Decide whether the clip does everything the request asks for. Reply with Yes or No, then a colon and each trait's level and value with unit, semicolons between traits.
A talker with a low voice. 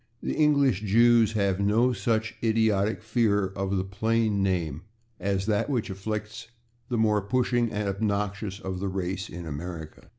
Yes: low, 105 Hz